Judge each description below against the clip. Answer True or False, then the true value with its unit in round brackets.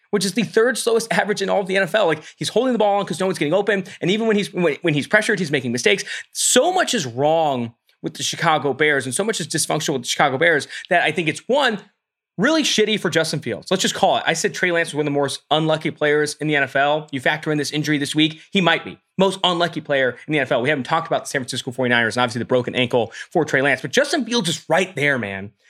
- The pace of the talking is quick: True (275 wpm)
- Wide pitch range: True (5.9 semitones)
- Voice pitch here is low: False (160 Hz)